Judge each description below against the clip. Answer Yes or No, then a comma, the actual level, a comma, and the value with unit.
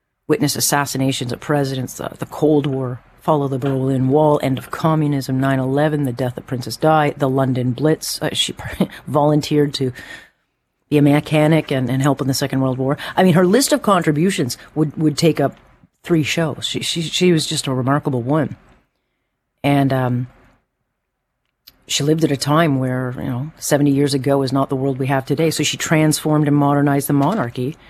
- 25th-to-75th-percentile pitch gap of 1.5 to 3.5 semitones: Yes, narrow, 2.4 semitones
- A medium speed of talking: Yes, average, 185 wpm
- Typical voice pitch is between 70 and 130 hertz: No, medium, 140 Hz